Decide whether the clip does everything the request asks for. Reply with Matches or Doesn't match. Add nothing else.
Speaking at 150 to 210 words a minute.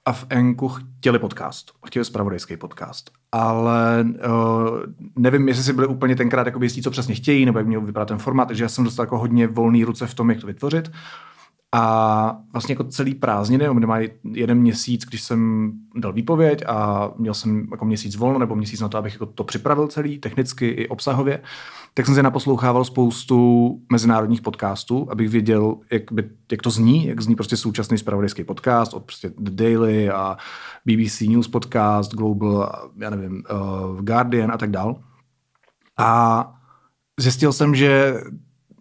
Matches